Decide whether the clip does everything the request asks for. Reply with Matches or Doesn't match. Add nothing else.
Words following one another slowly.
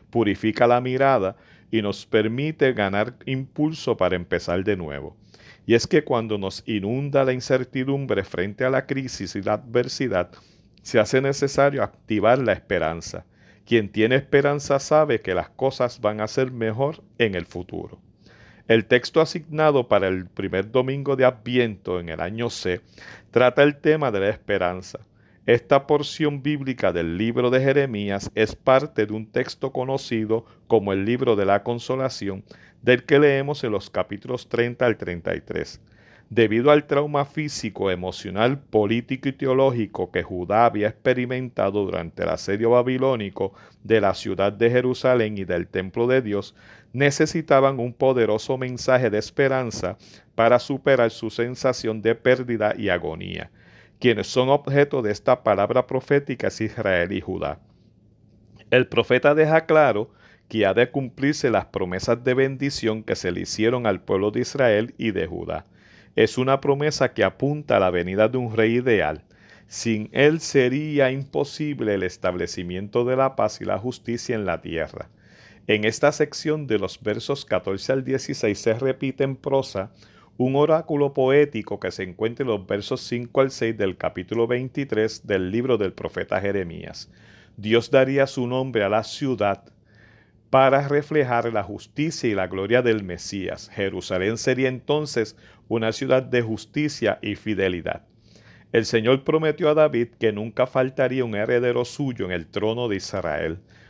Doesn't match